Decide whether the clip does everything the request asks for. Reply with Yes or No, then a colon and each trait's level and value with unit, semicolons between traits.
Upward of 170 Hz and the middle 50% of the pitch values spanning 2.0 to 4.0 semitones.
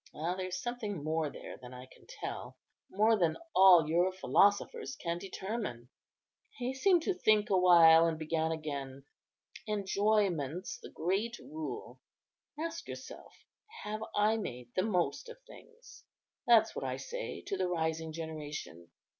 No: medium, 185 Hz; wide, 5.5 semitones